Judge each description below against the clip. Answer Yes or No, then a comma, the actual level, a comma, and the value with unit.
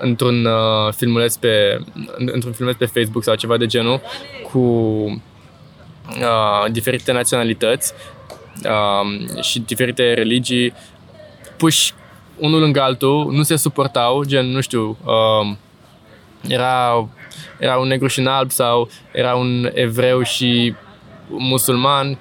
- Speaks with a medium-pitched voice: No, low, 125 Hz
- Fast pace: No, average, 120 wpm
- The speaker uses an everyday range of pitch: No, narrow, 2.1 semitones